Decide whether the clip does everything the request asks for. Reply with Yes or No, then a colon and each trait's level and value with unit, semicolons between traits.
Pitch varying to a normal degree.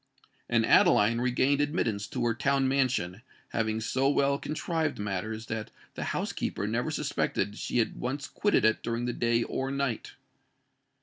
Yes: average, 3.7 semitones